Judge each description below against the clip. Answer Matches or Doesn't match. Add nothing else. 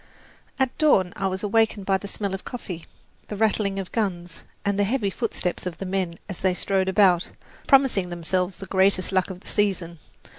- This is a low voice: Doesn't match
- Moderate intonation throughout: Doesn't match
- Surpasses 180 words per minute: Matches